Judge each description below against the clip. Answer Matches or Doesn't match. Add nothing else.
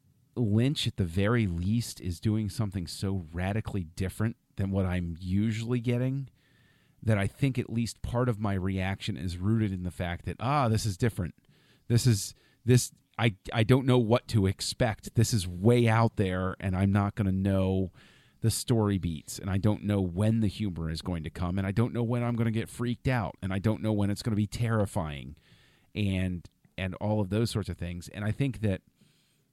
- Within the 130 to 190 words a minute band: Doesn't match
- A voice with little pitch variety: Doesn't match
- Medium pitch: Doesn't match